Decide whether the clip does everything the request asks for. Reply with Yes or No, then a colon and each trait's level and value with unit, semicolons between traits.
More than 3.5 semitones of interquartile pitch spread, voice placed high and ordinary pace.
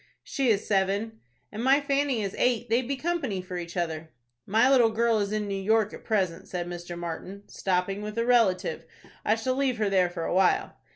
No: average, 4.4 semitones; high, 210 Hz; fast, 210 wpm